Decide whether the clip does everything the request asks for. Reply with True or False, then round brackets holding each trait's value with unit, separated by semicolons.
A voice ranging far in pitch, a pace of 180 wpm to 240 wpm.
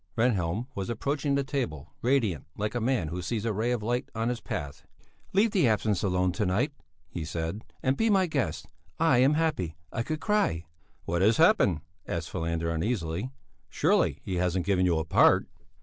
True (7.3 semitones; 185 wpm)